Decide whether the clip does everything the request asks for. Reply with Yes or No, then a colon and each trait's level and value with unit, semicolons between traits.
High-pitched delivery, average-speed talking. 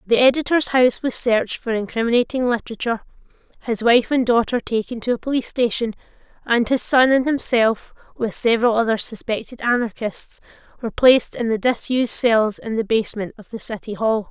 Yes: high, 235 Hz; average, 170 wpm